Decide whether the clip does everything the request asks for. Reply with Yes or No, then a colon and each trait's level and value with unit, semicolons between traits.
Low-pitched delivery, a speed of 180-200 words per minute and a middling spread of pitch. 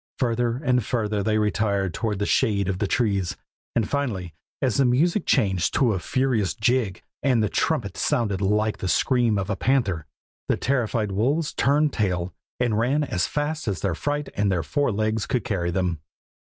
Yes: low, 110 Hz; average, 185 wpm; average, 4.7 semitones